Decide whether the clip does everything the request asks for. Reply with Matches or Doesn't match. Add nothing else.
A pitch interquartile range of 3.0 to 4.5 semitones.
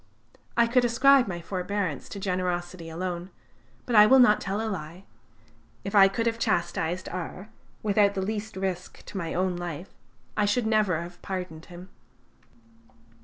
Matches